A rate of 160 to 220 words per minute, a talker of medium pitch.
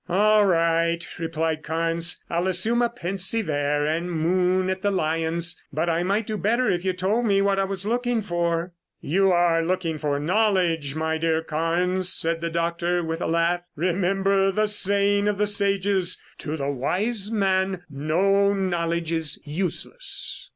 Yes: average, 165 wpm; medium, 180 Hz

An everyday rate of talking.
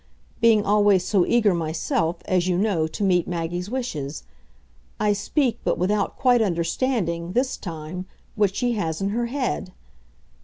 Yes: average, 150 wpm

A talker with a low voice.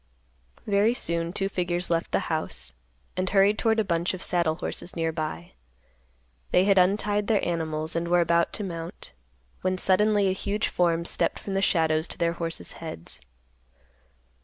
No: medium, 175 Hz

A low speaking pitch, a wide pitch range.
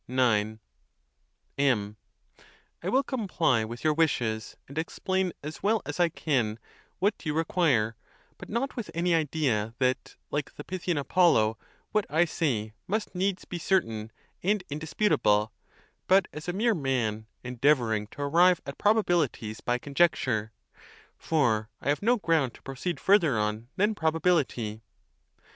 No: medium, 150 Hz; wide, 7.7 semitones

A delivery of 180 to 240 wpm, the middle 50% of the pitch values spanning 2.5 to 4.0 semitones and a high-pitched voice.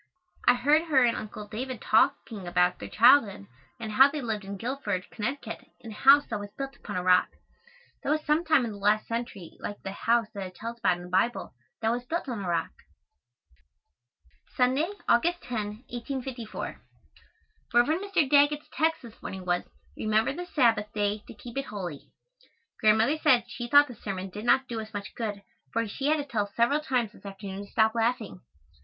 No: average, 195 wpm; average, 4.6 semitones; high, 230 Hz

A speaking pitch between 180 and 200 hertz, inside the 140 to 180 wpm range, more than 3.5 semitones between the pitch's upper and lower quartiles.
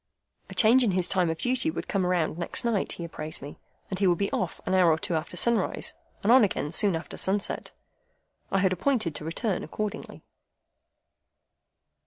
No: medium, 185 Hz; average, 195 wpm; average, 4.1 semitones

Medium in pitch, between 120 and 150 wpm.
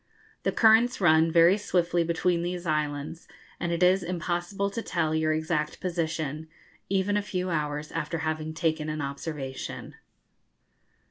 Yes: medium, 165 Hz; average, 140 wpm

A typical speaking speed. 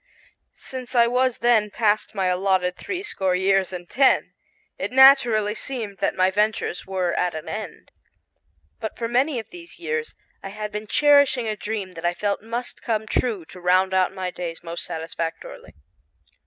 Yes: average, 170 wpm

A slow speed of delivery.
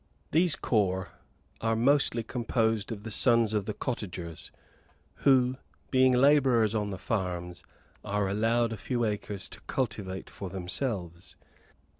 Yes: slow, 130 wpm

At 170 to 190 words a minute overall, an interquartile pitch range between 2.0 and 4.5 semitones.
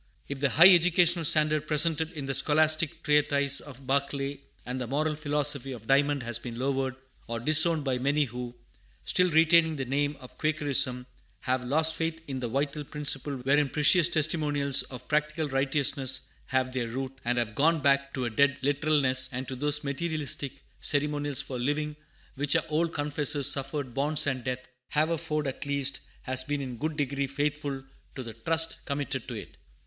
Yes: average, 175 wpm; narrow, 2.4 semitones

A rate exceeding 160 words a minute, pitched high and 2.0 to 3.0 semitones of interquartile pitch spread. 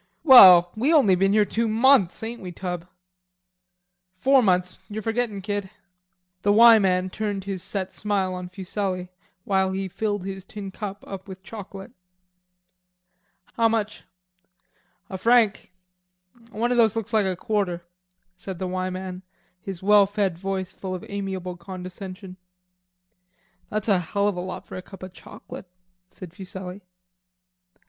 No: average, 150 wpm; high, 195 Hz; narrow, 2.4 semitones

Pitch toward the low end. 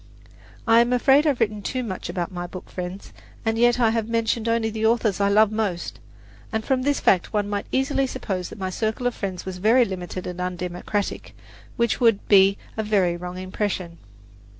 No: high, 210 Hz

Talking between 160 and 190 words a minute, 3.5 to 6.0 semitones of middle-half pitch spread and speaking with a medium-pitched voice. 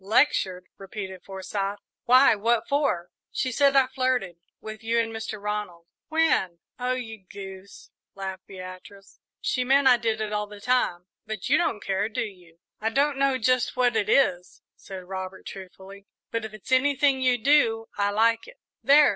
No: average, 170 wpm; average, 4.7 semitones; high, 220 Hz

